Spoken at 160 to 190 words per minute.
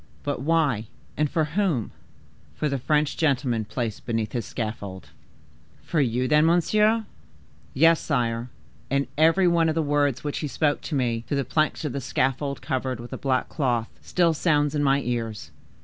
Yes: average, 175 wpm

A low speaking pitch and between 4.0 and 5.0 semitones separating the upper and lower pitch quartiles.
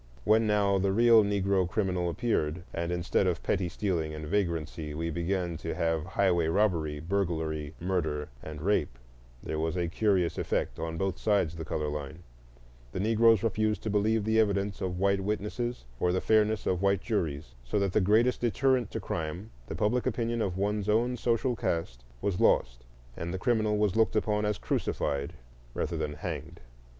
Yes: very low, 95 Hz; average, 4.3 semitones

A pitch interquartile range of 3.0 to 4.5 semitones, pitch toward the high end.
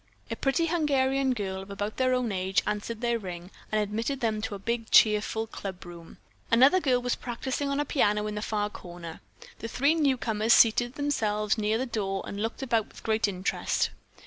Yes: average, 3.7 semitones; high, 220 Hz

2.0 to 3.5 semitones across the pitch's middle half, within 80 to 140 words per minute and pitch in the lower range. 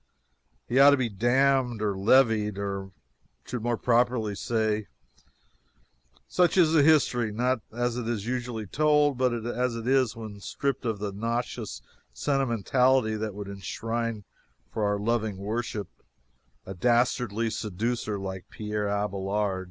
Yes: average, 3.1 semitones; slow, 135 wpm; low, 115 Hz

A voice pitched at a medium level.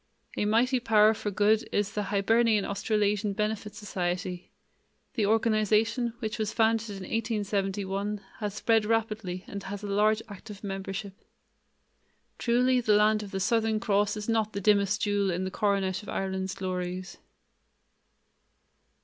No: high, 210 Hz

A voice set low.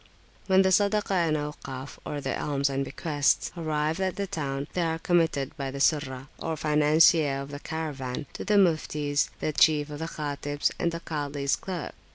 No: medium, 150 Hz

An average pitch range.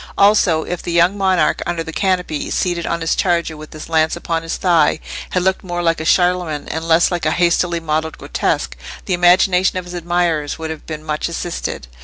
No: narrow, 1.9 semitones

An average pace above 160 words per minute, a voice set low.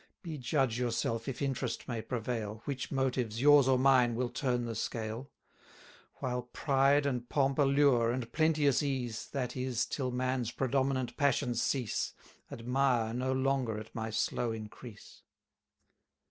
No: average, 140 wpm; low, 125 Hz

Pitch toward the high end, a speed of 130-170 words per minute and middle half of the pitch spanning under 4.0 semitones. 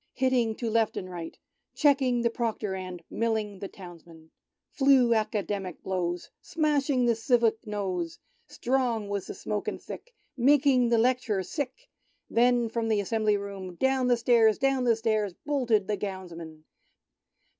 No: high, 225 Hz; average, 150 wpm; average, 4.3 semitones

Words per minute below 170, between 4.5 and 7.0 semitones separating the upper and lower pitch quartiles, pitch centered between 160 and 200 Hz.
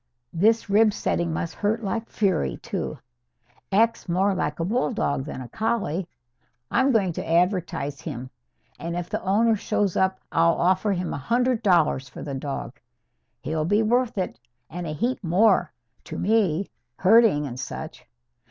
Yes: average, 160 wpm; average, 5.2 semitones; medium, 185 Hz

